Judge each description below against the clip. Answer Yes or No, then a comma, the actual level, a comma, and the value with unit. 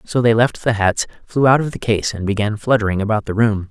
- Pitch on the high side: No, low, 110 Hz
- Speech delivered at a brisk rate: Yes, fast, 260 wpm